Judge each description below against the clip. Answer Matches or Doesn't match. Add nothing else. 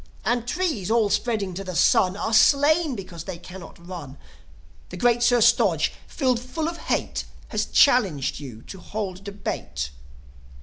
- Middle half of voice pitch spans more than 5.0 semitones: Matches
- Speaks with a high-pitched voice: Matches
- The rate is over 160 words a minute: Doesn't match